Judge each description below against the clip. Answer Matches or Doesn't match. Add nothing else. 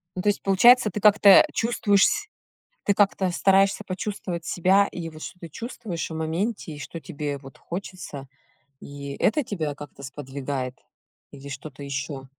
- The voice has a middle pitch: Matches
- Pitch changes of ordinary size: Doesn't match